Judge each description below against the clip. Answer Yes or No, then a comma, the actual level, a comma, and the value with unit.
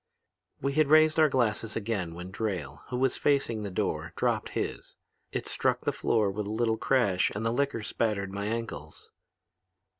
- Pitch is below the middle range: Yes, low, 110 Hz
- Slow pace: No, average, 175 wpm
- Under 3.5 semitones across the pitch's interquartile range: No, average, 4.6 semitones